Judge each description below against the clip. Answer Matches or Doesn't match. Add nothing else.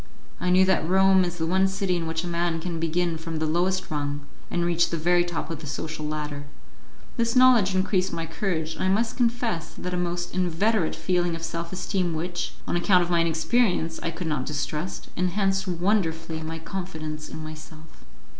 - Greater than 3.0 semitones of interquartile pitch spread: Doesn't match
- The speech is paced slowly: Doesn't match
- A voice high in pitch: Doesn't match